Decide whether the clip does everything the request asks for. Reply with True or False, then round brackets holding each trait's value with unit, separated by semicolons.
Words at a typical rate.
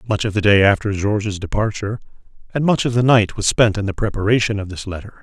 False (230 wpm)